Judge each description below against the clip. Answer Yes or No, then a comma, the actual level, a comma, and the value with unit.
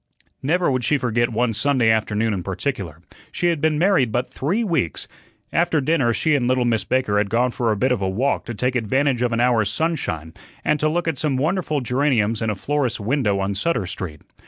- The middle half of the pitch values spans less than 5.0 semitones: No, average, 5.3 semitones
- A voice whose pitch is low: Yes, low, 125 Hz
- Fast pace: Yes, fast, 215 wpm